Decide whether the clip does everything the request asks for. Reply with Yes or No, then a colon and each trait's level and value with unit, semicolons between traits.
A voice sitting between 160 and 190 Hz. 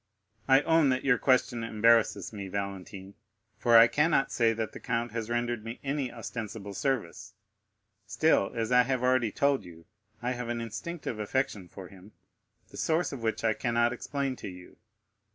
No: low, 115 Hz